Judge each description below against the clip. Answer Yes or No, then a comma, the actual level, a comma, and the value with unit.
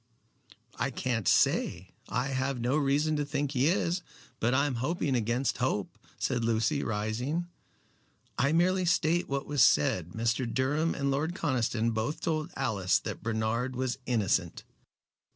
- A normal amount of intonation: Yes, average, 4.2 semitones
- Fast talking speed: No, average, 150 wpm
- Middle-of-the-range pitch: No, low, 130 Hz